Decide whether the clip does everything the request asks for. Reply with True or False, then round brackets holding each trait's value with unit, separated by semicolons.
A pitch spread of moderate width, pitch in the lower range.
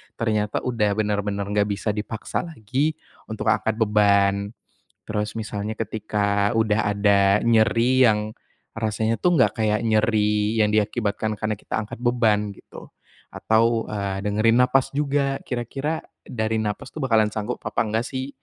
False (1.8 semitones; 110 Hz)